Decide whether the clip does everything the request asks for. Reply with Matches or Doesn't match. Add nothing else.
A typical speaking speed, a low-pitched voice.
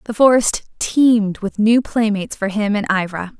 Doesn't match